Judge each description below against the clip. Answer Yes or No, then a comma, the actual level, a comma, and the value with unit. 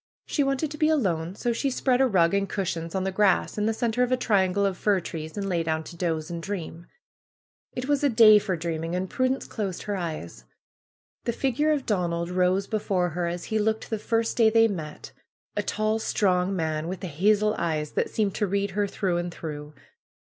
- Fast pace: Yes, fast, 210 wpm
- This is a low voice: No, high, 195 Hz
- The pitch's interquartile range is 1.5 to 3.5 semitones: No, average, 4.4 semitones